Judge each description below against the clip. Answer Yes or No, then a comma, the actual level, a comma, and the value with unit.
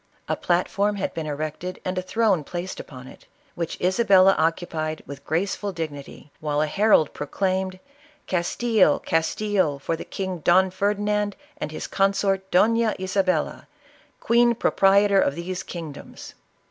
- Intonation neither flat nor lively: Yes, average, 3.9 semitones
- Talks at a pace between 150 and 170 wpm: No, average, 140 wpm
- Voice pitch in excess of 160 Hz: Yes, medium, 185 Hz